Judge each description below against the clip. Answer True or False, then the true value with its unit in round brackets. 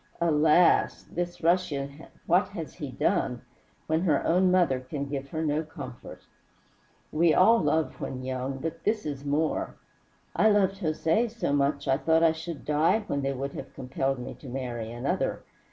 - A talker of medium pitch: True (150 Hz)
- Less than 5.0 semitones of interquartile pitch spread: True (3.7 semitones)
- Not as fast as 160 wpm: False (170 wpm)